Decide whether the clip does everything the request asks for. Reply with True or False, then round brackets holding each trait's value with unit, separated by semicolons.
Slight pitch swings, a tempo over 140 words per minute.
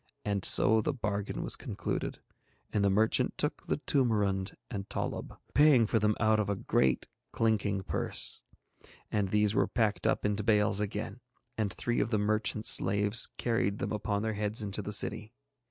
True (1.5 semitones; 170 wpm)